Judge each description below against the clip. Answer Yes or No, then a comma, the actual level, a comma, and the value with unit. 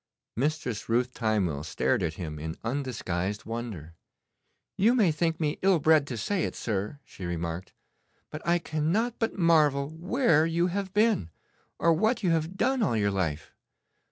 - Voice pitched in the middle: Yes, medium, 145 Hz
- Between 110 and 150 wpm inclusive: No, average, 160 wpm